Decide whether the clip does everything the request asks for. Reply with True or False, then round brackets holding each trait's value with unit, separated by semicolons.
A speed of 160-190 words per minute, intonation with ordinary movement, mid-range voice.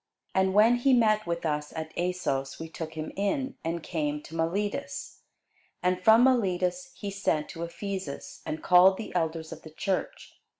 True (170 wpm; 4.1 semitones; 180 Hz)